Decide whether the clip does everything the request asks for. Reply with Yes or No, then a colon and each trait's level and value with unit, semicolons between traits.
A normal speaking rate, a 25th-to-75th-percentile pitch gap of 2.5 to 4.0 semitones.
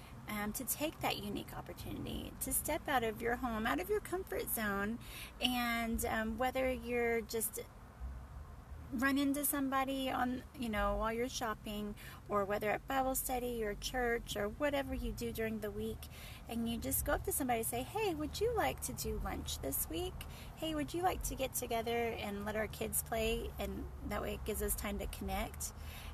Yes: average, 195 wpm; average, 3.5 semitones